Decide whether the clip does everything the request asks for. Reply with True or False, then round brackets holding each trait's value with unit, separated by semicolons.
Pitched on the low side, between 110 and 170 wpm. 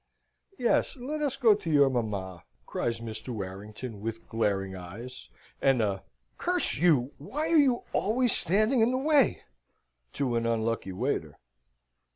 True (125 Hz; 145 wpm)